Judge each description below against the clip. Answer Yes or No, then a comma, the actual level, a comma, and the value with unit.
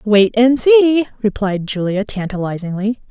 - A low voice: No, high, 220 Hz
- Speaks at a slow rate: Yes, slow, 115 wpm